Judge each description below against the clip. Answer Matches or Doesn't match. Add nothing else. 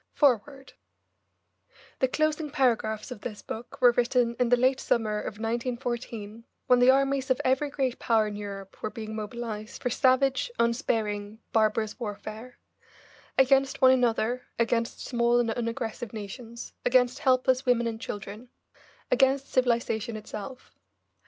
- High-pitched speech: Matches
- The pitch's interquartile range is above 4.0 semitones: Doesn't match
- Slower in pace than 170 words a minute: Matches